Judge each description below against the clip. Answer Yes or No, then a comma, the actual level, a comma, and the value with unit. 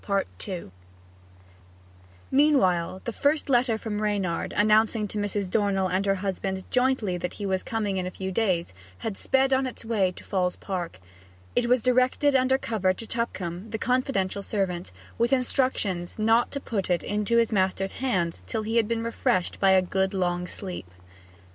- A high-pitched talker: Yes, high, 205 Hz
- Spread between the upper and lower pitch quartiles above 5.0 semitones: No, average, 3.9 semitones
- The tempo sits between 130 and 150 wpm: No, average, 165 wpm